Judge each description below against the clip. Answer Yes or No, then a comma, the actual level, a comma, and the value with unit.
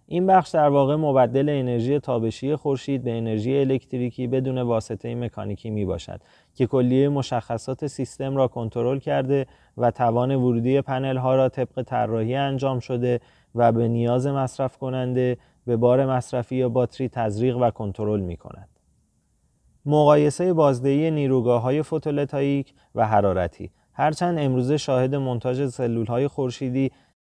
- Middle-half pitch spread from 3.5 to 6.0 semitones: No, narrow, 2.5 semitones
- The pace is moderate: Yes, average, 135 wpm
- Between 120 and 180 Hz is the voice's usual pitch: Yes, low, 130 Hz